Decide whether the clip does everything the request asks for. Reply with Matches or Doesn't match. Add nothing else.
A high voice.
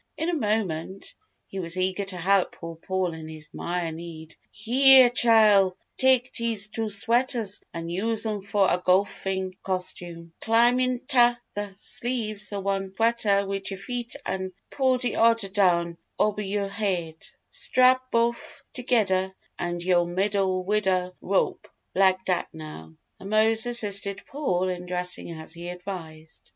Matches